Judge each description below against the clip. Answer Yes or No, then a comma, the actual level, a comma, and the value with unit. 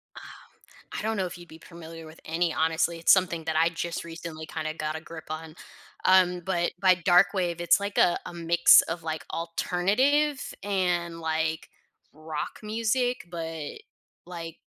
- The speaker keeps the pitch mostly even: Yes, narrow, 2.2 semitones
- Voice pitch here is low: No, medium, 170 Hz